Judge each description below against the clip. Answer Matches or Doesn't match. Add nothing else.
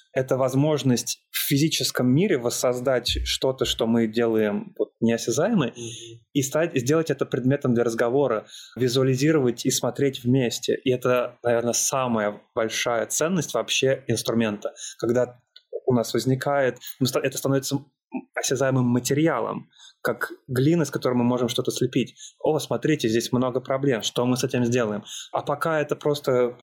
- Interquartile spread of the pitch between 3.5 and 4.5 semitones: Doesn't match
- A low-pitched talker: Matches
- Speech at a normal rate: Matches